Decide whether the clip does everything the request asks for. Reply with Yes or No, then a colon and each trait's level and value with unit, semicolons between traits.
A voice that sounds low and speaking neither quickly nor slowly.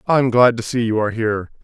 No: low, 115 Hz; fast, 255 wpm